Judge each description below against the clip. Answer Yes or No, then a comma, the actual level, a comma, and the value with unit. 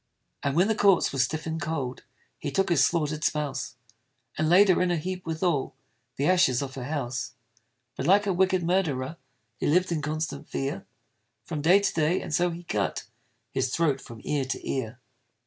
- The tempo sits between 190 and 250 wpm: Yes, average, 195 wpm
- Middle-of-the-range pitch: Yes, medium, 155 Hz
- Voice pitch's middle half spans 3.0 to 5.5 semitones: Yes, average, 4.5 semitones